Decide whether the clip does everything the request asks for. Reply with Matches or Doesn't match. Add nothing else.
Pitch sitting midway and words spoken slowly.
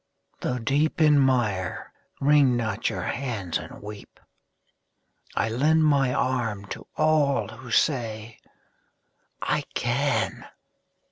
Doesn't match